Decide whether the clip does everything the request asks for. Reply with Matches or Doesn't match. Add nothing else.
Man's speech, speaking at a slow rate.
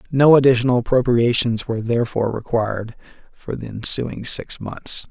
Matches